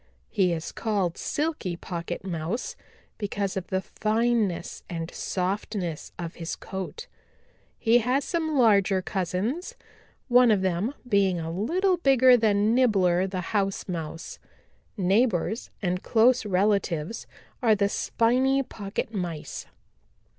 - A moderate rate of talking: No, slow, 120 wpm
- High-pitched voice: Yes, high, 200 Hz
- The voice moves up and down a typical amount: Yes, average, 4.8 semitones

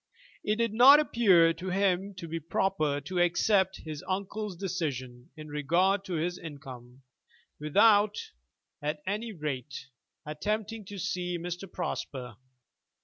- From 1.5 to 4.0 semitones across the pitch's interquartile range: No, average, 4.9 semitones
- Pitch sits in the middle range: Yes, medium, 180 Hz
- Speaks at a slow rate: Yes, slow, 130 wpm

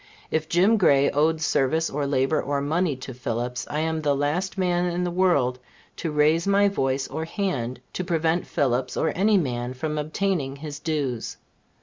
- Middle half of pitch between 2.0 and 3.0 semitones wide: No, average, 4.3 semitones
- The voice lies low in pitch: No, medium, 155 Hz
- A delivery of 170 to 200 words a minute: Yes, average, 180 wpm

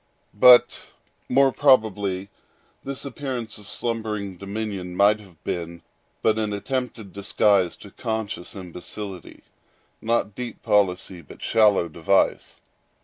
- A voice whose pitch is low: Yes, low, 105 Hz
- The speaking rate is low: Yes, slow, 100 wpm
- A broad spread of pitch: No, average, 3.2 semitones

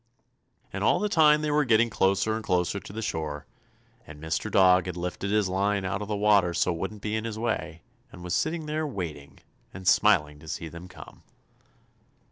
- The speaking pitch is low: Yes, low, 100 Hz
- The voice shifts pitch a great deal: No, average, 3.9 semitones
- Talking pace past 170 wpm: Yes, fast, 205 wpm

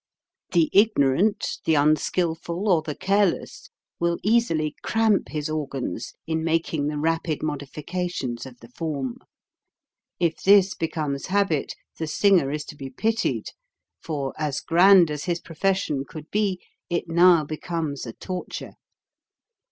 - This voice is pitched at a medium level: Yes, medium, 165 Hz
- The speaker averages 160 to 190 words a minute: No, slow, 135 wpm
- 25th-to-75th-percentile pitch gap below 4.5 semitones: Yes, average, 3.7 semitones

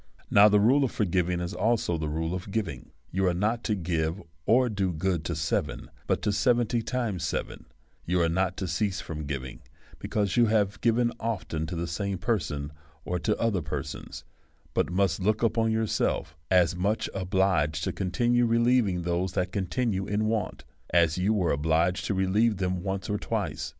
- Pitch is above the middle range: No, very low, 95 Hz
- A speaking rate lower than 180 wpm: No, average, 185 wpm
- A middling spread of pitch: Yes, average, 4.1 semitones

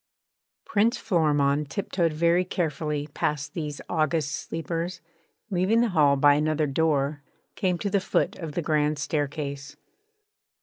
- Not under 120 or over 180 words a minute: Yes, slow, 135 wpm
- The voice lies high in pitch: No, medium, 155 Hz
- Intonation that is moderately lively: Yes, average, 3.1 semitones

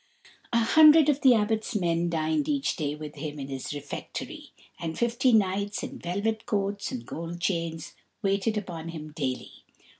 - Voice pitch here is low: No, medium, 185 Hz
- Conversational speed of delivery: Yes, average, 160 wpm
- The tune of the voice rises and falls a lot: Yes, wide, 5.9 semitones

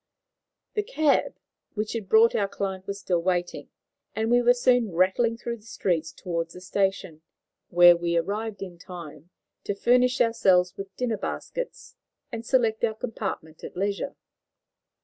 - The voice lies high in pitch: Yes, high, 200 Hz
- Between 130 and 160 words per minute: Yes, average, 150 wpm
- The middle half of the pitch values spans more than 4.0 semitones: Yes, average, 4.4 semitones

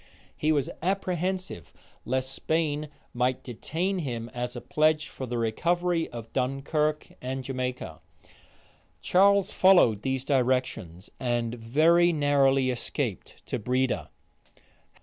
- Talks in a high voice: No, low, 135 Hz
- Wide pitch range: No, average, 4.7 semitones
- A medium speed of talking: No, slow, 110 wpm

